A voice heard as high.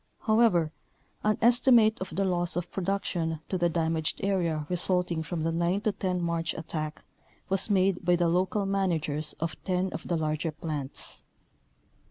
No: medium, 175 Hz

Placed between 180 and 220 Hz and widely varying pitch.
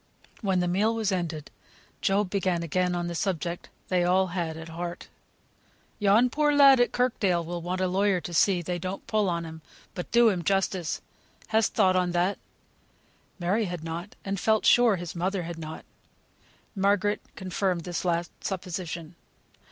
No: medium, 185 Hz; narrow, 2.6 semitones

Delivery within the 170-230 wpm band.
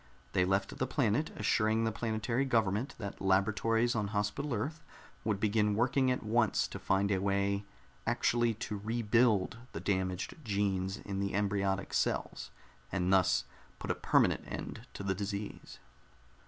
No: average, 150 wpm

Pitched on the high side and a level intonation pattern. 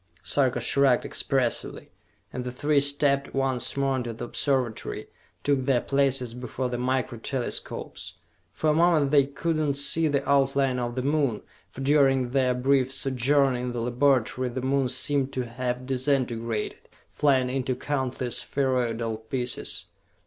No: low, 130 Hz; narrow, 2.0 semitones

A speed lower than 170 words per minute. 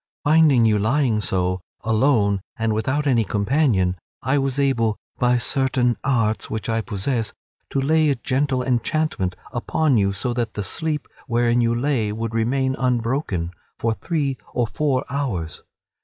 Yes: average, 150 wpm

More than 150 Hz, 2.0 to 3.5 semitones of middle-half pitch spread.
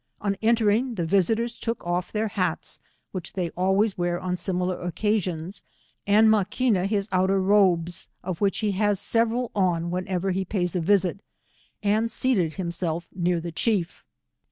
Yes: high, 190 Hz; average, 3.2 semitones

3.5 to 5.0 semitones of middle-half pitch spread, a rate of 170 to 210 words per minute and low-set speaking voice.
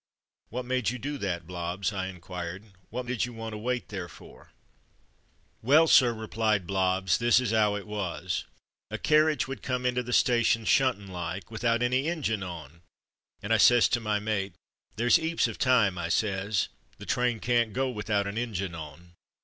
Yes: average, 4.5 semitones; average, 180 wpm; low, 110 Hz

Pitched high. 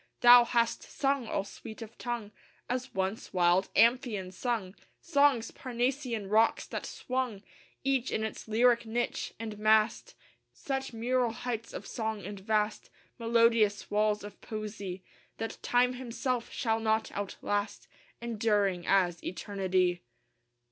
Yes: high, 225 Hz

